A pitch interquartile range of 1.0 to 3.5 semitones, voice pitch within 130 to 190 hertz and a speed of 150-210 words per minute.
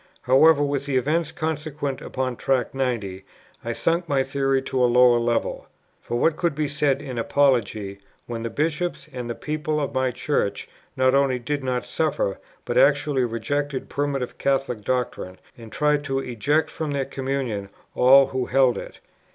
Yes: average, 2.9 semitones; low, 135 Hz; average, 165 wpm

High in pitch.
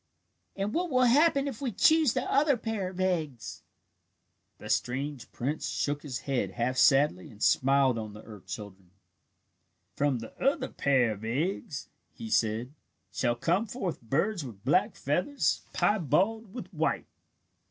No: medium, 145 Hz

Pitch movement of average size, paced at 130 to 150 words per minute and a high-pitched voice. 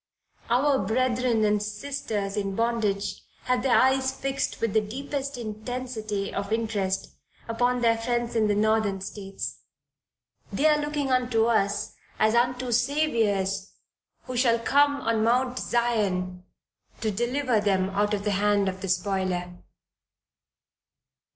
Yes: average, 3.8 semitones; slow, 135 wpm; high, 225 Hz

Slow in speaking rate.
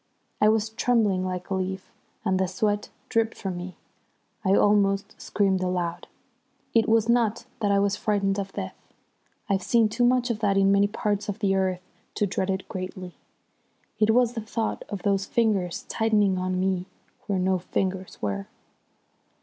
No: average, 170 wpm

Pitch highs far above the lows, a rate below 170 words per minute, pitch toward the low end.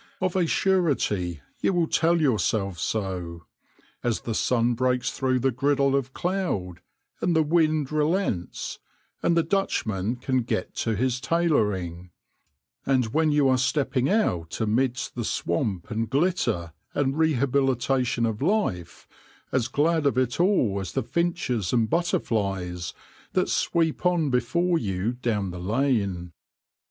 Yes: wide, 7.1 semitones; average, 140 wpm; low, 130 Hz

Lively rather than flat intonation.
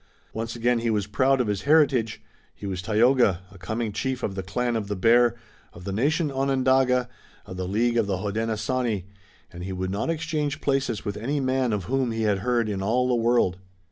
No: average, 4.2 semitones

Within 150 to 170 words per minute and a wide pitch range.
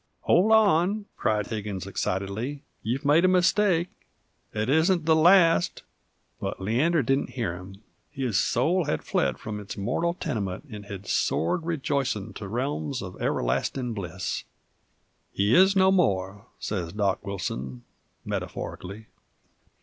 No: slow, 135 wpm; wide, 8.9 semitones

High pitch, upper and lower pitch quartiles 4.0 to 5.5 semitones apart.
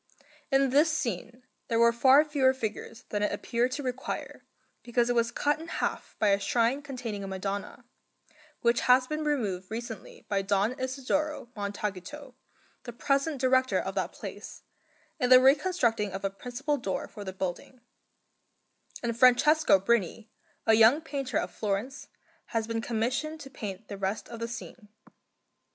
Yes: high, 240 Hz; average, 4.4 semitones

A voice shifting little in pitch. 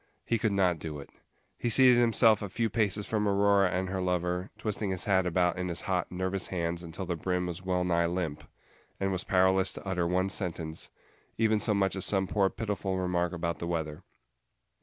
Yes: narrow, 2.2 semitones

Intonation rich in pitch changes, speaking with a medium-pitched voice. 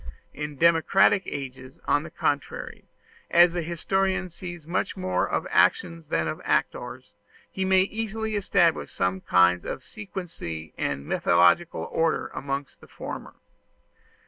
Yes: wide, 6.0 semitones; medium, 165 Hz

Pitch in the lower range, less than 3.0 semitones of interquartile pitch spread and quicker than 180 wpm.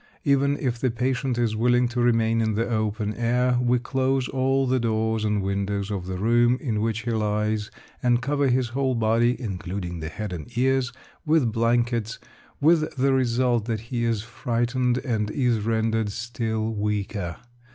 No: low, 115 Hz; narrow, 2.5 semitones; average, 170 wpm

